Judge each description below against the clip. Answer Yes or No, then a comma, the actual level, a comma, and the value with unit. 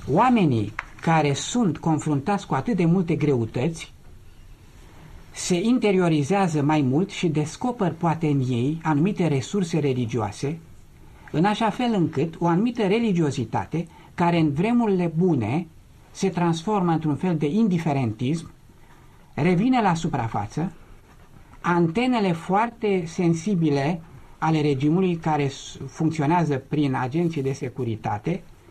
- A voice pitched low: No, medium, 160 Hz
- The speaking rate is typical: No, slow, 110 wpm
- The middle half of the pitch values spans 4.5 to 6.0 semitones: Yes, average, 4.8 semitones